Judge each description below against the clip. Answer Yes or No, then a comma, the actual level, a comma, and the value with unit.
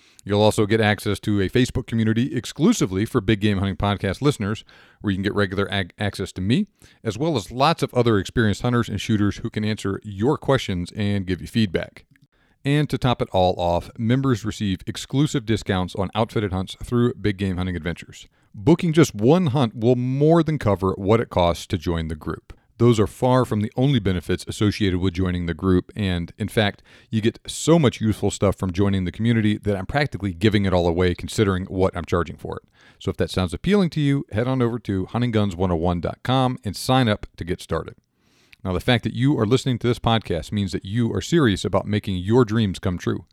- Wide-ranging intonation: No, average, 4.1 semitones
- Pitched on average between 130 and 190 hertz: No, low, 105 Hz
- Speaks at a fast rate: Yes, fast, 210 wpm